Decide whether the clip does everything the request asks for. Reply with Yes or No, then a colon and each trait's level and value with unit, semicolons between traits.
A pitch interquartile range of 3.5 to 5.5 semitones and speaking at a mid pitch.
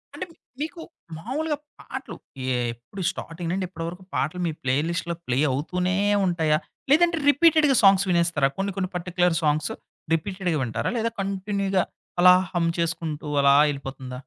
Yes: average, 4.0 semitones; medium, 180 Hz